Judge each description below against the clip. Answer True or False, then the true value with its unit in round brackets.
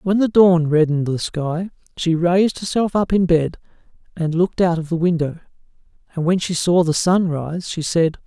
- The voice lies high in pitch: False (170 Hz)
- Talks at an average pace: True (195 wpm)